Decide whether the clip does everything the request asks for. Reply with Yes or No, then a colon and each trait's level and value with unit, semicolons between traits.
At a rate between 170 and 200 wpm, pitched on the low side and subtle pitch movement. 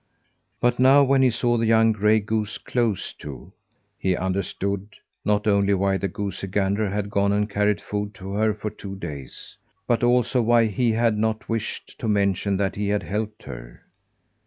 Yes: average, 180 wpm; low, 105 Hz; narrow, 2.2 semitones